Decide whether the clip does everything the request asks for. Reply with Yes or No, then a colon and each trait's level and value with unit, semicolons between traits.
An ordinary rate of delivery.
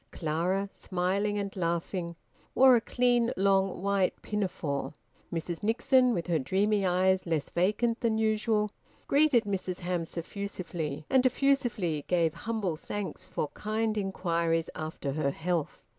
No: slow, 130 wpm